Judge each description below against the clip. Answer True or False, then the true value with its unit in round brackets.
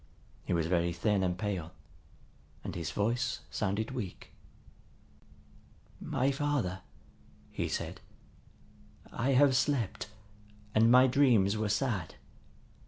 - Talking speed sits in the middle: False (105 wpm)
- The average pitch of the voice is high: False (110 Hz)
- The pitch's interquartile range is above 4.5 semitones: True (5.5 semitones)